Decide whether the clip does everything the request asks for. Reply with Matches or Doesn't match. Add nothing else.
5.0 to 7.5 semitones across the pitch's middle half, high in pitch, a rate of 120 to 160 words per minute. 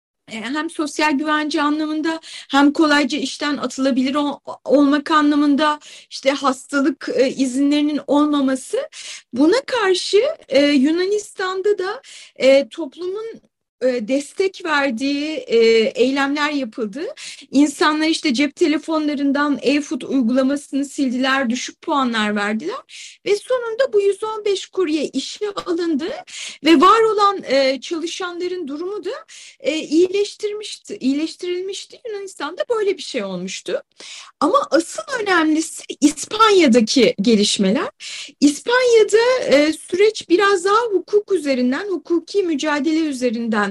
Doesn't match